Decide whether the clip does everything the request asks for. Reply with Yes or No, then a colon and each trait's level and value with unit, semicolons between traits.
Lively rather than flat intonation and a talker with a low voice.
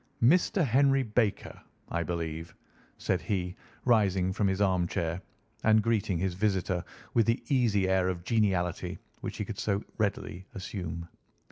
No: average, 3.7 semitones; very low, 95 Hz